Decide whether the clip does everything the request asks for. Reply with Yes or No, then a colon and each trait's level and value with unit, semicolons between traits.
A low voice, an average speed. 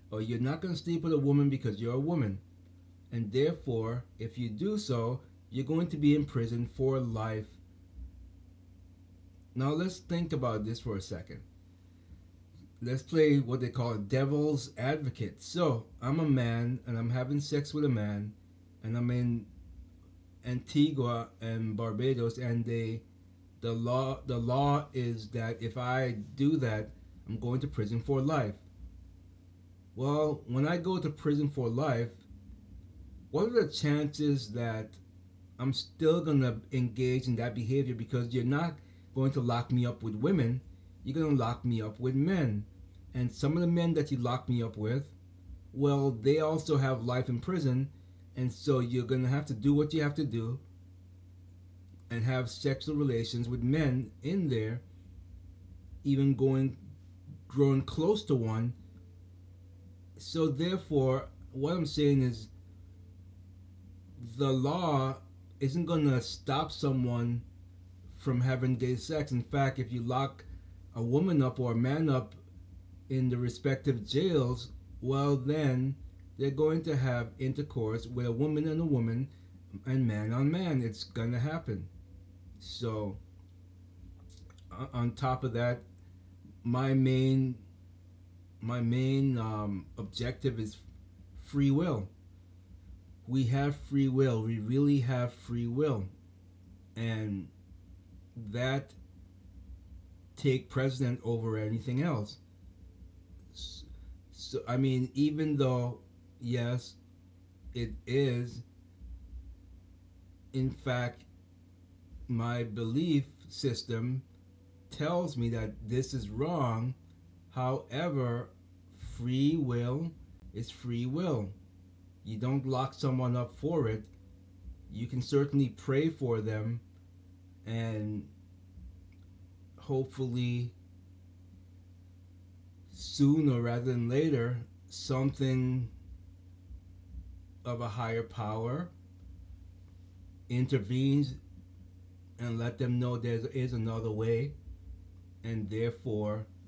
No: low, 115 Hz; slow, 125 wpm